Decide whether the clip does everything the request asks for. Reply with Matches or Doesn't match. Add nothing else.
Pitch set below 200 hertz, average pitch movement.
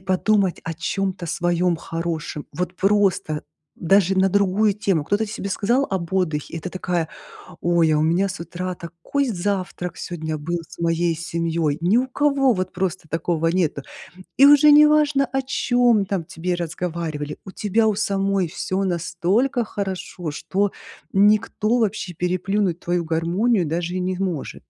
Matches